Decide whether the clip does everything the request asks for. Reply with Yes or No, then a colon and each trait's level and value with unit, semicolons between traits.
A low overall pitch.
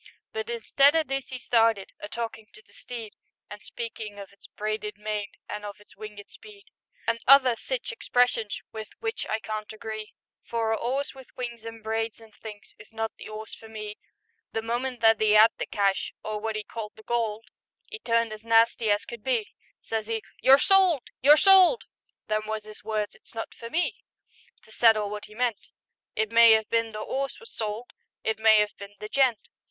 No: high, 225 Hz